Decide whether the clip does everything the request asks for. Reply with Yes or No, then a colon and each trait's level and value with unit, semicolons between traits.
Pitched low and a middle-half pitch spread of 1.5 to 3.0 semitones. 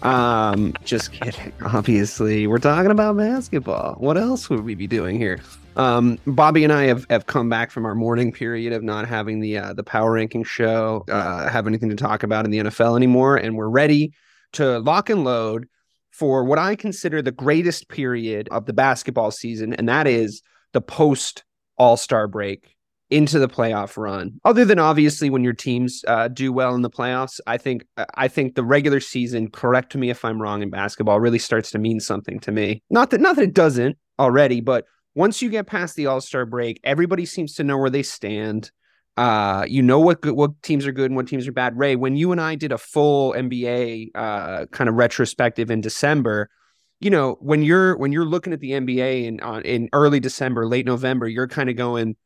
No: low, 125 Hz; average, 4.4 semitones